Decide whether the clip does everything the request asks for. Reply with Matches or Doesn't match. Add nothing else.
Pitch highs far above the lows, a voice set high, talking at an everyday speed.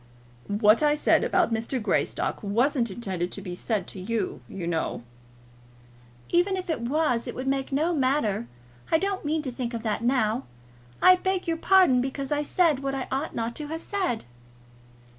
Matches